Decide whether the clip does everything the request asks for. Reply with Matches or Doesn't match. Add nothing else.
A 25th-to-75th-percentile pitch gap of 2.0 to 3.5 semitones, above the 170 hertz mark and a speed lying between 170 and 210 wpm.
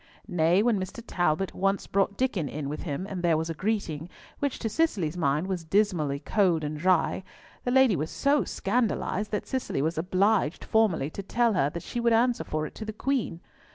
Doesn't match